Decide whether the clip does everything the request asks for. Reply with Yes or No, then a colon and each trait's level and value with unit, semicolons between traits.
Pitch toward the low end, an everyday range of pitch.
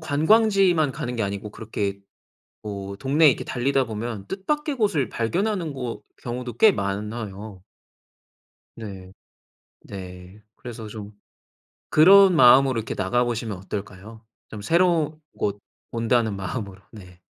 No: low, 115 Hz; wide, 6.8 semitones